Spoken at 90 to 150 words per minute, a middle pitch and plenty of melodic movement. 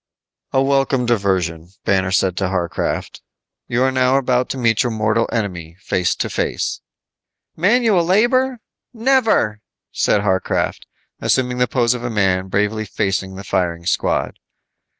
No: average, 140 wpm; low, 110 Hz; wide, 5.7 semitones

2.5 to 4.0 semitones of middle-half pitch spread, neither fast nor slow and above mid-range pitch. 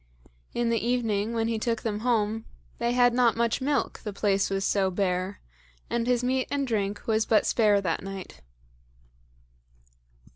Yes: average, 2.9 semitones; average, 160 wpm; high, 225 Hz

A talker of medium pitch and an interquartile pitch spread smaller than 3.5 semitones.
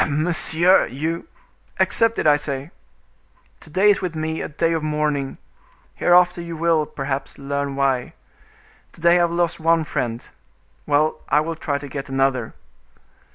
Yes: medium, 155 Hz; average, 3.1 semitones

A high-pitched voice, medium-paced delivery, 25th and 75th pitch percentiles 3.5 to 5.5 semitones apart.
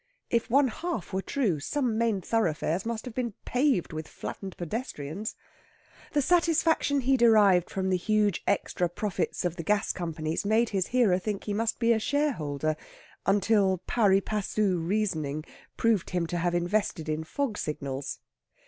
Yes: high, 205 Hz; average, 155 wpm; average, 5.0 semitones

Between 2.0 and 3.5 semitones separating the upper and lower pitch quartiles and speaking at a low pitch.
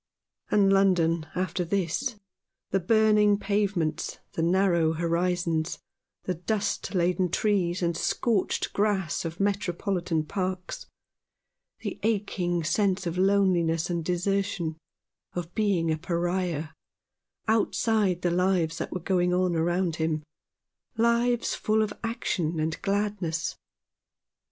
No: average, 3.0 semitones; medium, 180 Hz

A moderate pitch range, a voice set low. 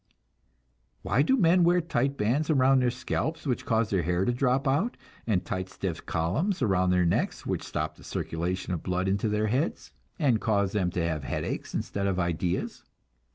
No: wide, 6.9 semitones; low, 105 Hz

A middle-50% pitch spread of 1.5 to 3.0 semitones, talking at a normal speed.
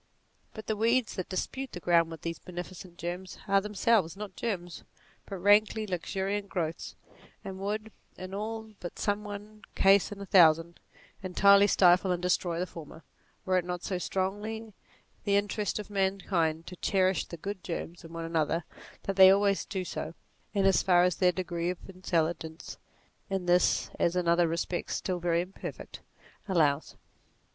Yes: narrow, 2.6 semitones; average, 170 wpm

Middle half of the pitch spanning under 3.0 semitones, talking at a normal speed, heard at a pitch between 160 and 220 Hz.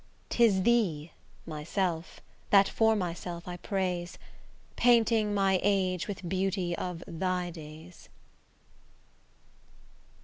No: narrow, 2.5 semitones; slow, 95 wpm; medium, 185 Hz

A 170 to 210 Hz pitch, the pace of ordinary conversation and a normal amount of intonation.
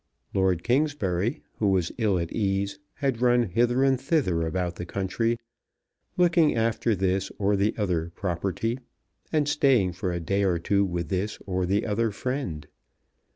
No: low, 100 Hz; average, 155 wpm; average, 4.9 semitones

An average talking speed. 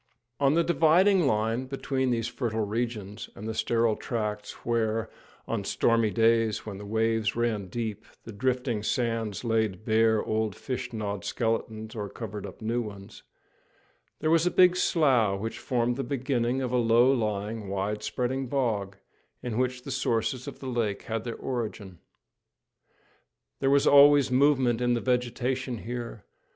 Yes: average, 155 wpm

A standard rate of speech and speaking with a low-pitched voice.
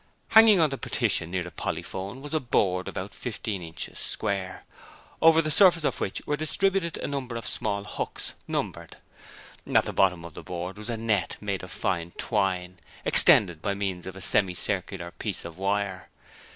Yes: average, 180 wpm; low, 100 Hz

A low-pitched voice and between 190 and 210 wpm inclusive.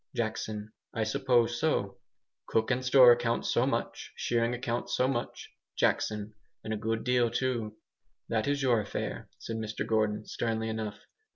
No: low, 115 Hz; average, 155 wpm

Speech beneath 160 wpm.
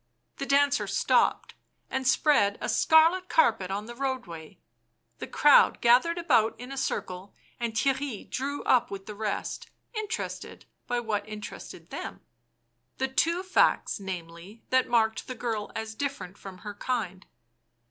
Yes: average, 145 wpm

